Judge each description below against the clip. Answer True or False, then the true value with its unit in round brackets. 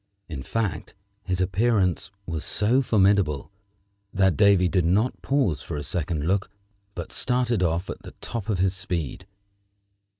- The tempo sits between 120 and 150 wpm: True (145 wpm)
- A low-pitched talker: True (95 Hz)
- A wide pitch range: False (3.7 semitones)